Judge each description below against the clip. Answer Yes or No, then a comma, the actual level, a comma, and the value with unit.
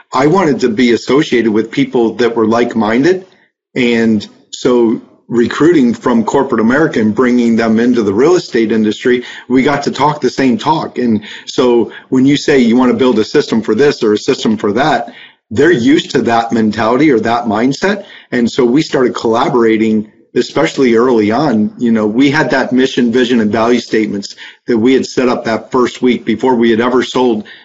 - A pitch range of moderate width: No, narrow, 2.3 semitones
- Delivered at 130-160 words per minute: No, average, 195 wpm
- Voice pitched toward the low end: Yes, low, 120 Hz